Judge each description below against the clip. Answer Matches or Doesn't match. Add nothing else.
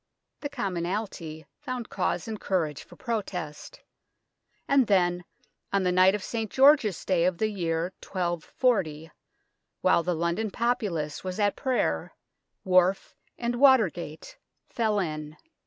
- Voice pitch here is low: Doesn't match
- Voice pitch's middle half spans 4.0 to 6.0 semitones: Matches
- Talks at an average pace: Doesn't match